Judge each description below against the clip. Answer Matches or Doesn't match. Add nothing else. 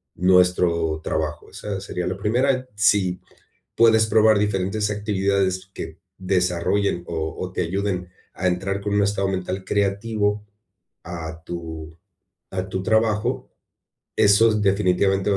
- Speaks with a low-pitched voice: Matches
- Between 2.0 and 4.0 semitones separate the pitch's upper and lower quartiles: Matches